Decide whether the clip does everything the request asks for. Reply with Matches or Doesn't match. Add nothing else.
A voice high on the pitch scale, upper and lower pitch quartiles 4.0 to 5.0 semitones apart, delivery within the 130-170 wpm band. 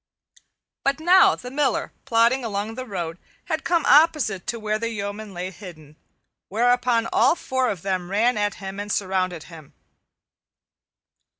Matches